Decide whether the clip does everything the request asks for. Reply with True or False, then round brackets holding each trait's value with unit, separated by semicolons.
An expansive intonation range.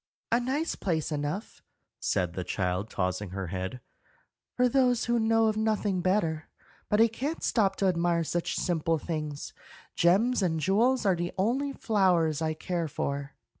True (6.6 semitones)